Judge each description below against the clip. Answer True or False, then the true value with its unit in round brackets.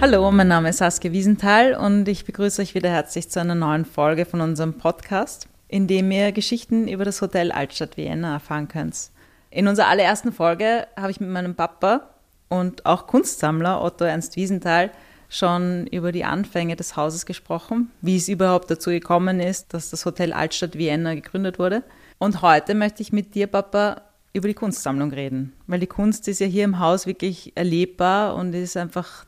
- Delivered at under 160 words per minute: False (180 wpm)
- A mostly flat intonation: False (3.2 semitones)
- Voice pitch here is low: False (180 Hz)